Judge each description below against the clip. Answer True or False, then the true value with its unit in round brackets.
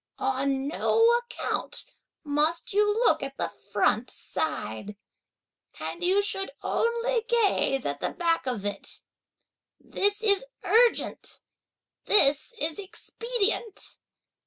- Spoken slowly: True (110 wpm)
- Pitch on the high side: True (390 Hz)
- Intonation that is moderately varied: False (8.5 semitones)